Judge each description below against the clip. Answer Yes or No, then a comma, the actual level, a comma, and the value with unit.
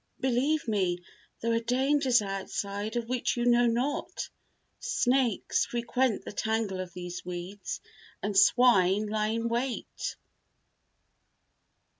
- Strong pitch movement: No, average, 3.8 semitones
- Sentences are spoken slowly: Yes, slow, 115 wpm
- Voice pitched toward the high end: Yes, high, 230 Hz